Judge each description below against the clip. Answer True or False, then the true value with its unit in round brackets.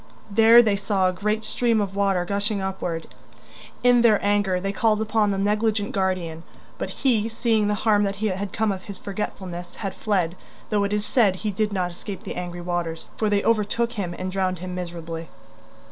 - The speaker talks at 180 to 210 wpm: True (190 wpm)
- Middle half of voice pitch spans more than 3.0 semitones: False (2.7 semitones)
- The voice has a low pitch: False (200 Hz)